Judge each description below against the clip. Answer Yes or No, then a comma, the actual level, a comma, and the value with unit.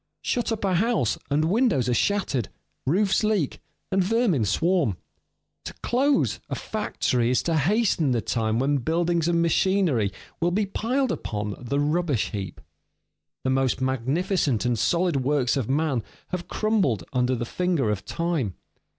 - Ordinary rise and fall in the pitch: No, wide, 7.2 semitones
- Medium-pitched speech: Yes, medium, 155 Hz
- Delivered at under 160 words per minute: Yes, average, 150 wpm